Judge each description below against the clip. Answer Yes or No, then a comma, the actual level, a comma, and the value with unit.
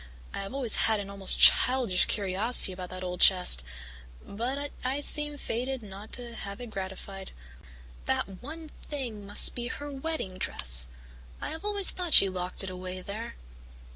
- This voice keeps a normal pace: Yes, average, 170 wpm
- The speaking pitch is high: Yes, high, 215 Hz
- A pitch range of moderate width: No, wide, 5.9 semitones